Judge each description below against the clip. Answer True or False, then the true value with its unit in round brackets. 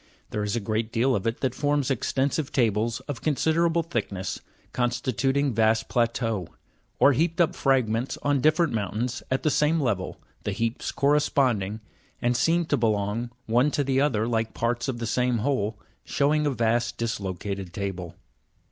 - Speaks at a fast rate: False (170 wpm)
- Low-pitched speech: True (120 Hz)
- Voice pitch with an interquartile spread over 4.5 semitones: False (4.2 semitones)